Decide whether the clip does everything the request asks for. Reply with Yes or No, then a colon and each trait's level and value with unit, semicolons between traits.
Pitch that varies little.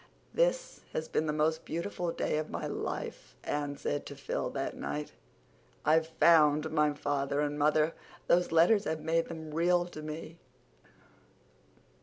Yes: narrow, 1.9 semitones